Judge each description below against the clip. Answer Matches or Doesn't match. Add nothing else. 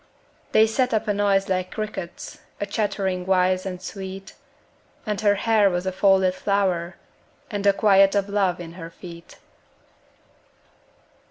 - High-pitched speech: Matches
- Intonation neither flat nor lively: Doesn't match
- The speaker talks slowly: Doesn't match